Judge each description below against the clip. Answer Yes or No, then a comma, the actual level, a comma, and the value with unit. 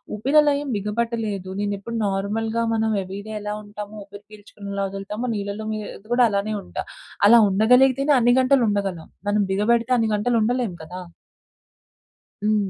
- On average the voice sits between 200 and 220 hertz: Yes, high, 210 Hz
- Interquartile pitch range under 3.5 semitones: Yes, average, 2.7 semitones